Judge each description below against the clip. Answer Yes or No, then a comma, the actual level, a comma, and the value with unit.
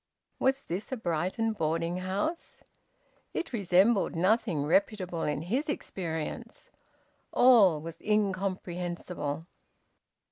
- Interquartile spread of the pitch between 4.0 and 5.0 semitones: Yes, average, 4.5 semitones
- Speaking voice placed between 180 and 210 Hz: Yes, medium, 185 Hz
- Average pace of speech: No, slow, 95 wpm